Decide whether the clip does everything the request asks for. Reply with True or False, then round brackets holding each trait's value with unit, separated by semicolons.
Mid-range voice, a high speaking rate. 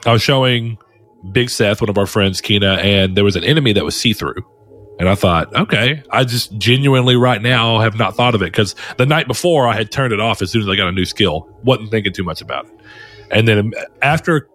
False (110 Hz; 245 wpm)